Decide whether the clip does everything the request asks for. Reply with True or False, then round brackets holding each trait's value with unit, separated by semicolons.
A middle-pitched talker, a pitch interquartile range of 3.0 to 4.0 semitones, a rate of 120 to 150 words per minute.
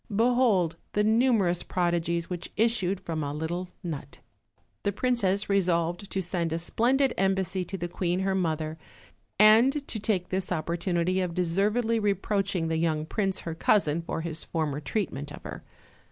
False (180 Hz; 3.6 semitones; 160 wpm)